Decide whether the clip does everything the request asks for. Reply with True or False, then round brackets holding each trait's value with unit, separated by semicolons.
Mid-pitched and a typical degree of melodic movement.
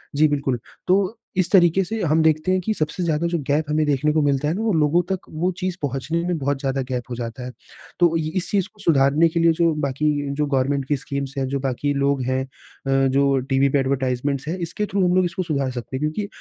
True (150 Hz; 3.8 semitones)